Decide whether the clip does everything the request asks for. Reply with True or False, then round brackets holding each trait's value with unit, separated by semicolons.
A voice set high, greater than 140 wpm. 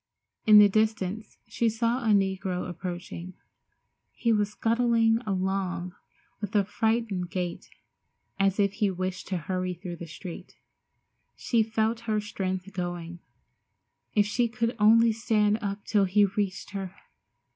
False (205 Hz; 135 wpm)